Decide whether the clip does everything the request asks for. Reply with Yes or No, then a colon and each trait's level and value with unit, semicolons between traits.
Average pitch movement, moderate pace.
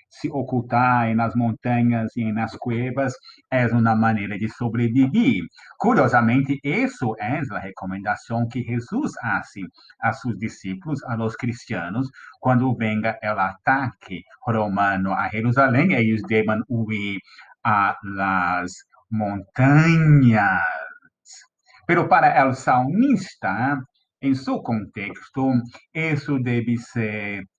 No: average, 3.4 semitones; slow, 105 wpm